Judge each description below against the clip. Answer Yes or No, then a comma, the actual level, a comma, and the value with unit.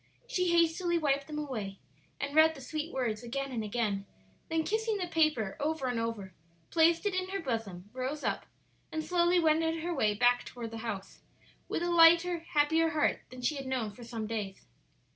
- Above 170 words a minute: Yes, average, 190 wpm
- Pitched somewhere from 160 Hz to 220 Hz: No, very high, 290 Hz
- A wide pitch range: Yes, wide, 6.1 semitones